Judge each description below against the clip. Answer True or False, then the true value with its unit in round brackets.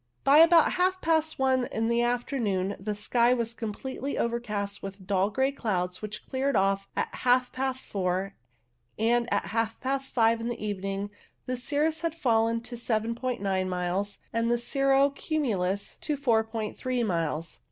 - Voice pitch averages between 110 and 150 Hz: False (230 Hz)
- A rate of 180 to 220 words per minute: False (155 wpm)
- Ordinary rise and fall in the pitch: True (4.6 semitones)